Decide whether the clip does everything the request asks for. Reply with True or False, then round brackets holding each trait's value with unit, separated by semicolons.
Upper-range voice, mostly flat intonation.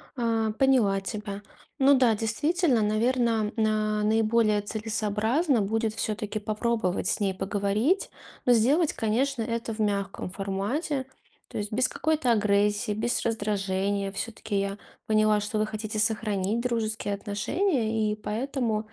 True (215 Hz; 2.2 semitones)